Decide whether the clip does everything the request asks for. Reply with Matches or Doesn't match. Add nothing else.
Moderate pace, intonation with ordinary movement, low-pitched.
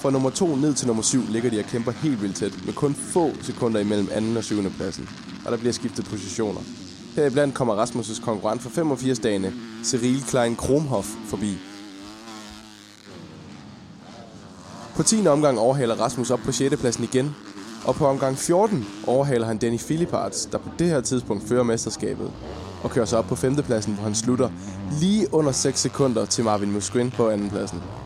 Matches